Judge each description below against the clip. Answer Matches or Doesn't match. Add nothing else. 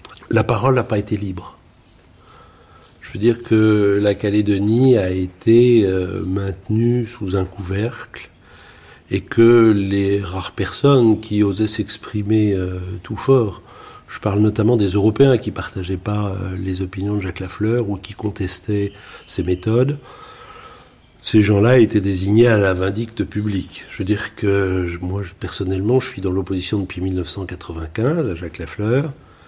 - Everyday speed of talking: Doesn't match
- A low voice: Matches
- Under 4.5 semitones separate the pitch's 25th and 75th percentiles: Matches